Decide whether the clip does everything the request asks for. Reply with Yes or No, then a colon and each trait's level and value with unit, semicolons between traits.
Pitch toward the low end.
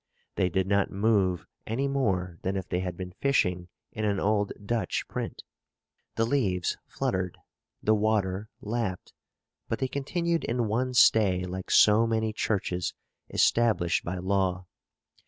Yes: low, 100 Hz